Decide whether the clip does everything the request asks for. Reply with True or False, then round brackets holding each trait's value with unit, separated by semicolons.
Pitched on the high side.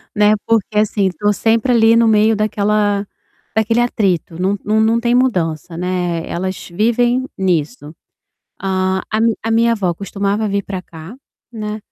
True (210 Hz)